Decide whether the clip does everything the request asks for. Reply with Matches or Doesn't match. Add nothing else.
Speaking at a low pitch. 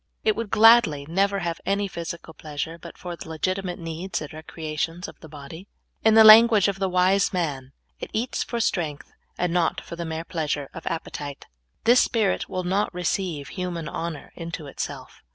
Doesn't match